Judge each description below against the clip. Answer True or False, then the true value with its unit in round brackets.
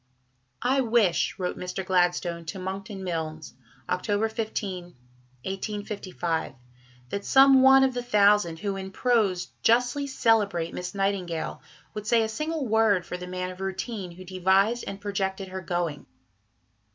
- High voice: True (195 Hz)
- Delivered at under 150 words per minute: True (140 wpm)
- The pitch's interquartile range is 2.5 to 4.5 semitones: True (3.7 semitones)